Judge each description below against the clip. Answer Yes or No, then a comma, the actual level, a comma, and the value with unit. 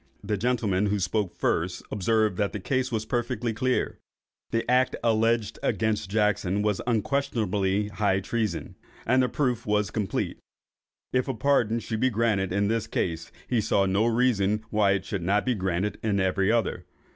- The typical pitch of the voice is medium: No, low, 105 Hz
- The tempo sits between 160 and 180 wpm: Yes, average, 170 wpm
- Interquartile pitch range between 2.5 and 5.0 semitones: Yes, average, 2.9 semitones